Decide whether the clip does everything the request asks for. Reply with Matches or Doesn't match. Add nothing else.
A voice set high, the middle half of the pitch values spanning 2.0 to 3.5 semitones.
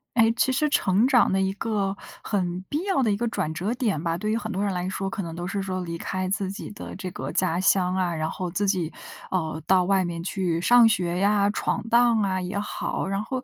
Matches